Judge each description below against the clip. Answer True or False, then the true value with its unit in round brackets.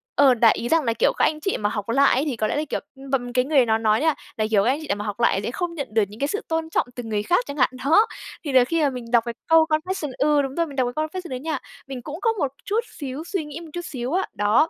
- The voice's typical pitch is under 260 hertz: False (275 Hz)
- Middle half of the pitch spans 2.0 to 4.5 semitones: False (5.1 semitones)